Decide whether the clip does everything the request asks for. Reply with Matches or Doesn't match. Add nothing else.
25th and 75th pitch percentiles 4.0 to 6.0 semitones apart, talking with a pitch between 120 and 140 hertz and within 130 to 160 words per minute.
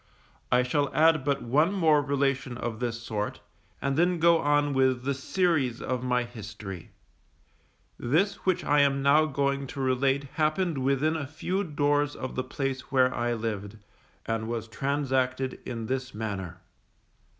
Doesn't match